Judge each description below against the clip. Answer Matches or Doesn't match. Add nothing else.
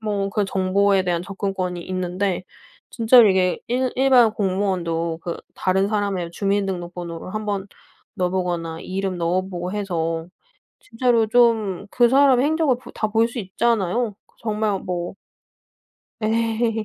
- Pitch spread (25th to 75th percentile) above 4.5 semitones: Doesn't match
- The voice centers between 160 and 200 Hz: Matches